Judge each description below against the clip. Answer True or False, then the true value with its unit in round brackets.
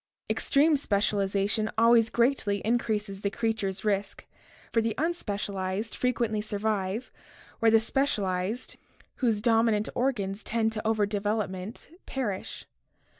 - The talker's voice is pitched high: True (215 Hz)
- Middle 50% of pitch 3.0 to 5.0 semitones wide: False (2.4 semitones)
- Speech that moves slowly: True (110 wpm)